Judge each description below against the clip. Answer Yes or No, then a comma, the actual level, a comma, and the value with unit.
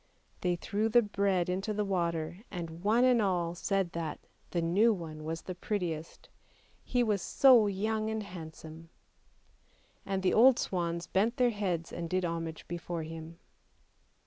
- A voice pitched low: No, medium, 180 Hz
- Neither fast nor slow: Yes, average, 160 wpm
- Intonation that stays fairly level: No, average, 4.0 semitones